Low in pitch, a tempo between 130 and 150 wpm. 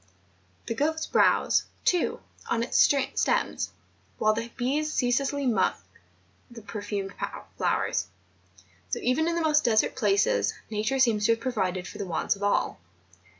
No: high, 230 Hz; average, 145 wpm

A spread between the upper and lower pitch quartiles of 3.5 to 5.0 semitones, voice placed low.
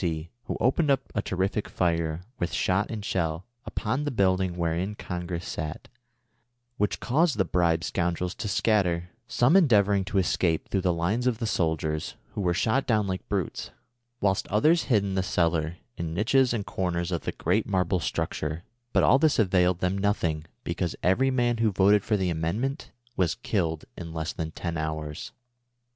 Yes: average, 4.0 semitones; very low, 95 Hz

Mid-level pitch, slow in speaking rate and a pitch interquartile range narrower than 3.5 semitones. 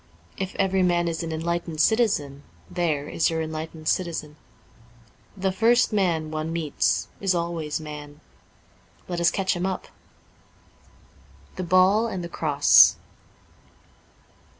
Yes: medium, 170 Hz; slow, 125 wpm; average, 3.0 semitones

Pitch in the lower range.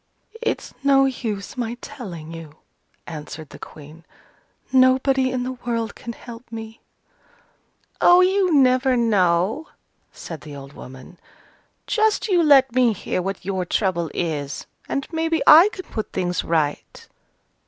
No: high, 230 Hz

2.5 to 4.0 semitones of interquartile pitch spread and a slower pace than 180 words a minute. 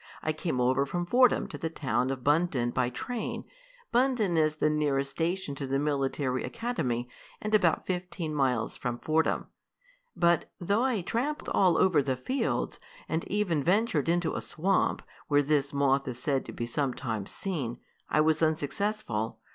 No: average, 5.2 semitones; average, 165 wpm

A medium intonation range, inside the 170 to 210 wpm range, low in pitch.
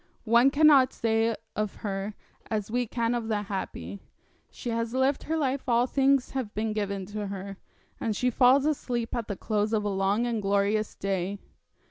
No: average, 3.5 semitones; average, 180 wpm; high, 225 Hz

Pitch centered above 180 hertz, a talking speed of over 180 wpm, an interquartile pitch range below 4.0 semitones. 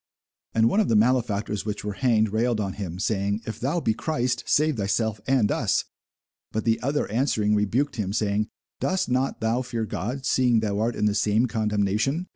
No: low, 110 Hz; average, 190 wpm; average, 3.3 semitones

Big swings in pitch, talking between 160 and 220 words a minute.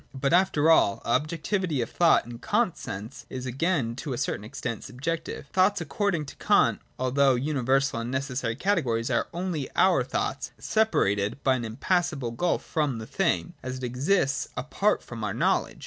Yes: wide, 5.8 semitones; average, 170 wpm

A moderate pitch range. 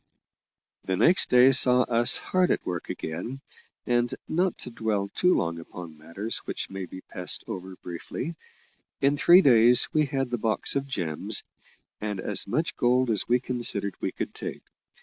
No: wide, 6.1 semitones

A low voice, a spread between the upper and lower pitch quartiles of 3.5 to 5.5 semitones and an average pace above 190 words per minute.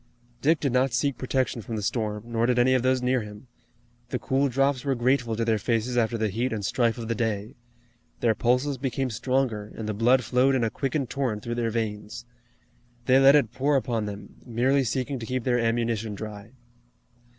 No: low, 120 Hz; average, 2.7 semitones; fast, 205 wpm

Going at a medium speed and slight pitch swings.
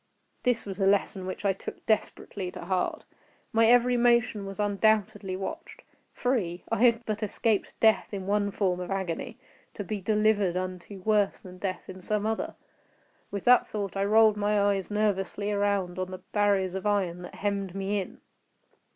Yes: average, 170 wpm; narrow, 2.1 semitones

